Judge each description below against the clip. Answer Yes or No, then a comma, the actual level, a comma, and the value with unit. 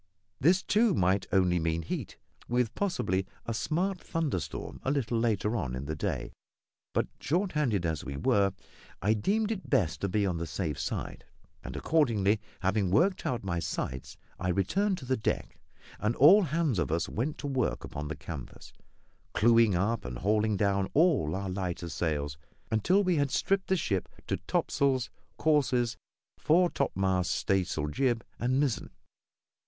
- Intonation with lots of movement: Yes, wide, 8.2 semitones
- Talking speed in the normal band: Yes, average, 165 wpm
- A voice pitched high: No, low, 110 Hz